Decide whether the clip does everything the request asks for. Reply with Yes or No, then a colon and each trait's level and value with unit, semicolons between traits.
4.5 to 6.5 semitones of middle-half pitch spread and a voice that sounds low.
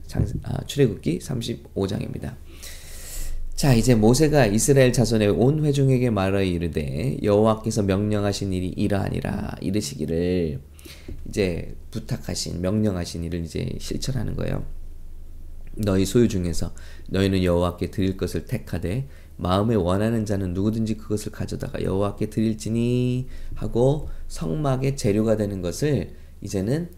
Yes: average, 5.3 semitones; very low, 95 Hz